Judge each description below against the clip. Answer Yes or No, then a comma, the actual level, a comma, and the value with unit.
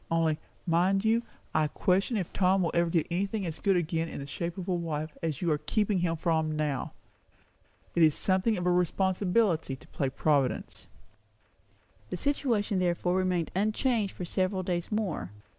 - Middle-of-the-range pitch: Yes, medium, 180 Hz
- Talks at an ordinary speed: Yes, average, 175 wpm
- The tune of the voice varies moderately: Yes, average, 3.2 semitones